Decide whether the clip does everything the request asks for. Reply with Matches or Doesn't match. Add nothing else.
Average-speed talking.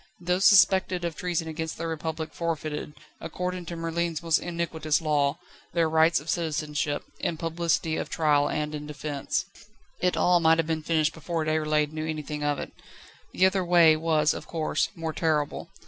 Matches